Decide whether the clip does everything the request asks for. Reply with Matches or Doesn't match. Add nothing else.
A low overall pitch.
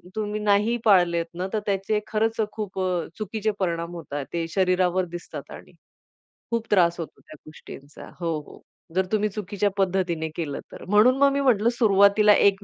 Doesn't match